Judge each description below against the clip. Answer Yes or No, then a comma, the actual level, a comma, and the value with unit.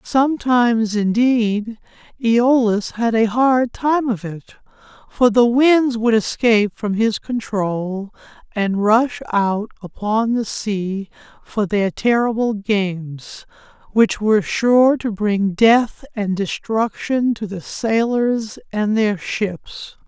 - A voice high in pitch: Yes, high, 220 Hz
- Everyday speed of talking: No, slow, 125 wpm